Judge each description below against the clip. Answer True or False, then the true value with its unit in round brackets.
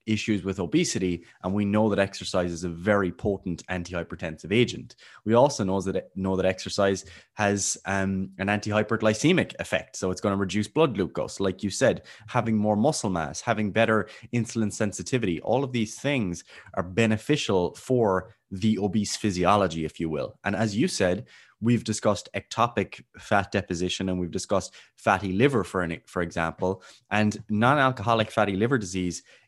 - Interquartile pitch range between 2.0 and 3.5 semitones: True (3.0 semitones)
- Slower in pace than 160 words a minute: False (165 wpm)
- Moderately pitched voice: False (100 Hz)